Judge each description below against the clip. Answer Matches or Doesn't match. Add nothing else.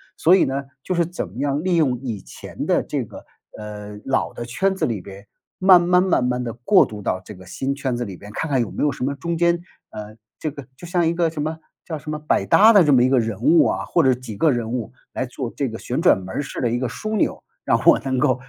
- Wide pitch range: Matches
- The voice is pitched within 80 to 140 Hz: Matches